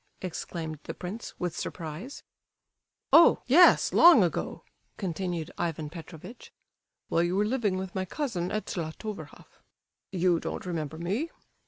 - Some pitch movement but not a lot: Yes, average, 4.2 semitones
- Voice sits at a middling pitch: Yes, medium, 180 Hz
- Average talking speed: No, slow, 130 wpm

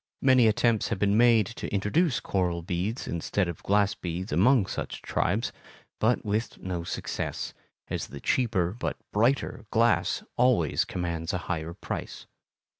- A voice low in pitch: Yes, low, 100 Hz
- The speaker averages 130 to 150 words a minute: Yes, average, 145 wpm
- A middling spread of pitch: Yes, average, 4.9 semitones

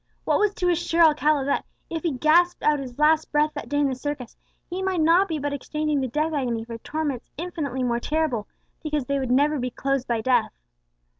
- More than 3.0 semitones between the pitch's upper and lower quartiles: Yes, average, 3.6 semitones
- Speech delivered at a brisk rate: Yes, fast, 215 wpm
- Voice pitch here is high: Yes, very high, 295 Hz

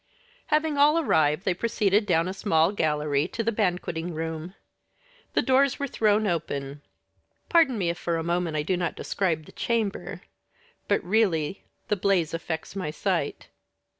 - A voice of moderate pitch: Yes, medium, 180 Hz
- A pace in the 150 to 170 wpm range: Yes, average, 160 wpm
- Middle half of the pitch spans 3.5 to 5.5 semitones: Yes, average, 5.0 semitones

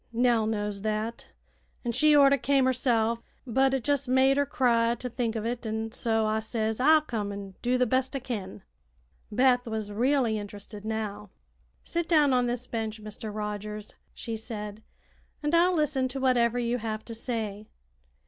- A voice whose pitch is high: Yes, high, 235 Hz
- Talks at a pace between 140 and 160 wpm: No, average, 175 wpm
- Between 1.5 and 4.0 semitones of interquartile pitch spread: Yes, average, 3.1 semitones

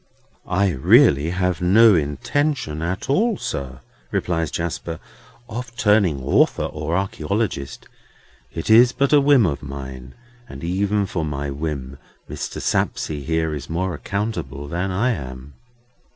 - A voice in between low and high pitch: No, very low, 85 Hz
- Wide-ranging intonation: Yes, wide, 6.3 semitones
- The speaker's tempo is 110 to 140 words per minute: Yes, slow, 135 wpm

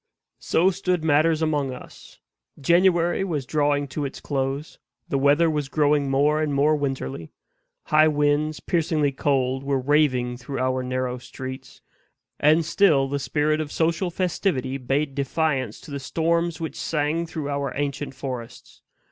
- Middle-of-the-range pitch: Yes, medium, 145 Hz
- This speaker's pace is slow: No, average, 150 wpm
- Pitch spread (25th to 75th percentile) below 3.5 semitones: Yes, average, 2.8 semitones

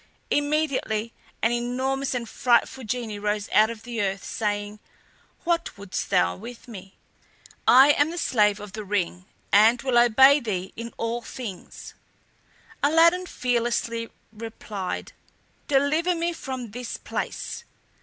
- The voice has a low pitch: No, high, 235 Hz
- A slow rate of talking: Yes, slow, 130 wpm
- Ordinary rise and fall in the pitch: Yes, average, 4.3 semitones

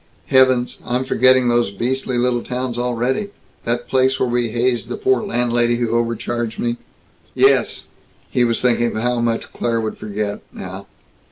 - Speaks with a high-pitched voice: No, low, 120 Hz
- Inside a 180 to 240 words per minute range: No, average, 160 wpm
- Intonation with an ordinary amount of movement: No, narrow, 1.3 semitones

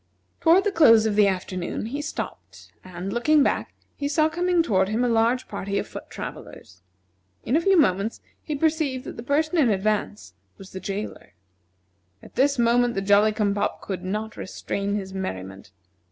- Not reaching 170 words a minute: No, average, 175 wpm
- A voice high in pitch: Yes, high, 220 Hz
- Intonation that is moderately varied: No, wide, 6.8 semitones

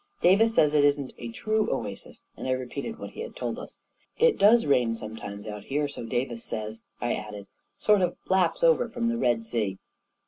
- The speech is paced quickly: Yes, fast, 215 wpm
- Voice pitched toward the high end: No, low, 135 Hz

